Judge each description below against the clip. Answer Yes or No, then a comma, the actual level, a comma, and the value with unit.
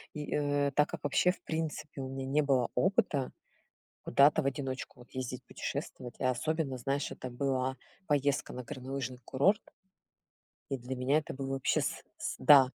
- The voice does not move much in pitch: Yes, narrow, 2.2 semitones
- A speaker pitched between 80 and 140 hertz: Yes, low, 135 Hz